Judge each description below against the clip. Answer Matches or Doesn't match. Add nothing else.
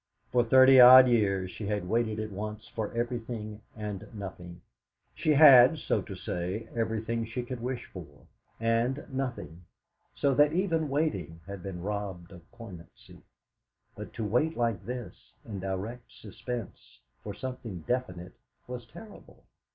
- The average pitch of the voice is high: Doesn't match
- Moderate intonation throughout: Matches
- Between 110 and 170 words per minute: Matches